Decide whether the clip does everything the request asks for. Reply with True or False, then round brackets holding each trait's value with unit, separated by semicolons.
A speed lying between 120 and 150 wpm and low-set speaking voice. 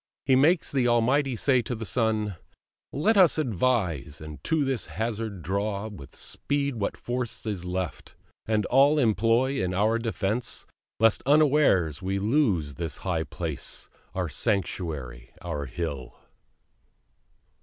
True (135 wpm; 110 Hz)